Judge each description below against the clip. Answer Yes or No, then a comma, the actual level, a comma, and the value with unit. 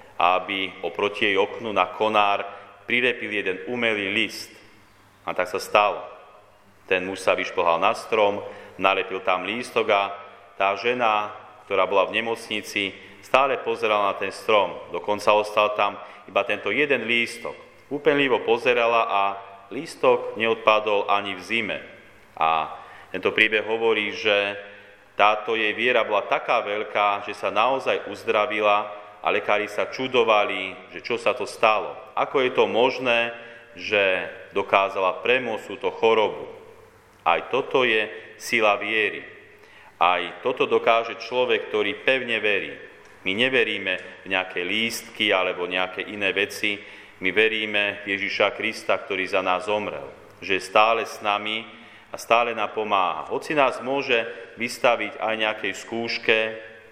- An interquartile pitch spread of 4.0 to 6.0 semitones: No, average, 2.7 semitones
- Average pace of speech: Yes, average, 135 wpm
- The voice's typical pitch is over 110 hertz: No, low, 105 Hz